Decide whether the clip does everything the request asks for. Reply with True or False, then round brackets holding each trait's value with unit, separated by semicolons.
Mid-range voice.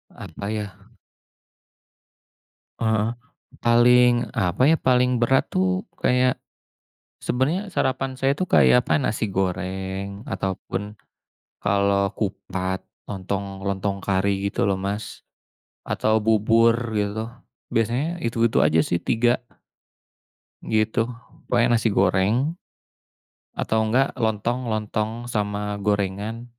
False (110 Hz)